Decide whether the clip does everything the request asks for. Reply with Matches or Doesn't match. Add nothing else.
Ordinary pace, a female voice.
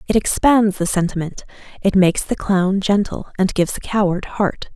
Matches